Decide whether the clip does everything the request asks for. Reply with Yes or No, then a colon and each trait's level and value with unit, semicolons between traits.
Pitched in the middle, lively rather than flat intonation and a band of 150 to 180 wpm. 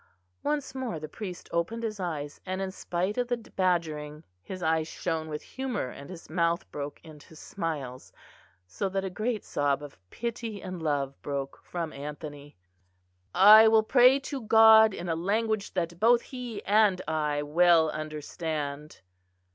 Yes: medium, 175 Hz; wide, 6.2 semitones; average, 155 wpm